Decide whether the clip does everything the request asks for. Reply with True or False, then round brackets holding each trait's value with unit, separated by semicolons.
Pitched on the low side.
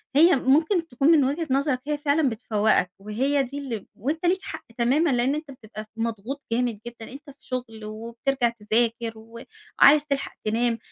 False (255 Hz)